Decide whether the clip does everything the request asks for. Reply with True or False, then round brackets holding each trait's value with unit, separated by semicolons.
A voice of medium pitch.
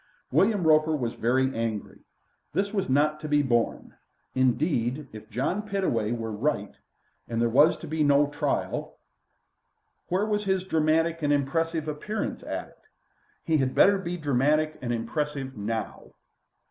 True (145 Hz)